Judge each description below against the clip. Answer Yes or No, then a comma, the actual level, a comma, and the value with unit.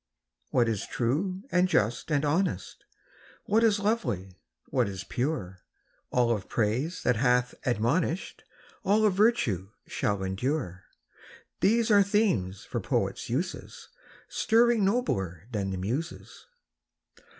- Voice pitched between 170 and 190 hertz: No, low, 130 Hz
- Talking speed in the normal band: No, slow, 130 wpm